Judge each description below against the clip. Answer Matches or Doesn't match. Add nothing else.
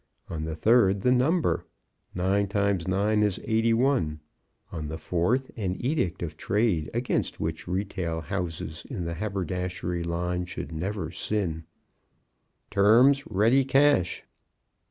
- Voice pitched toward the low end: Matches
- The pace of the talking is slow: Matches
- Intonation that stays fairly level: Doesn't match